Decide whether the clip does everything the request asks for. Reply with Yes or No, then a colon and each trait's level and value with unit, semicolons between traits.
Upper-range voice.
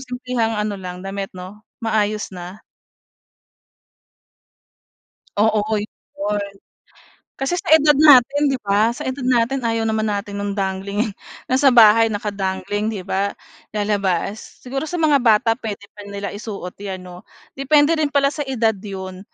Yes: high, 215 Hz